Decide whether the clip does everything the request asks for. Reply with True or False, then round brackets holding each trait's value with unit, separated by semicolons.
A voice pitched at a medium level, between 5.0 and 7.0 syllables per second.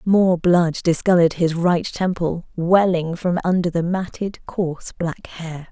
False (175 Hz; 4.1 syllables/s)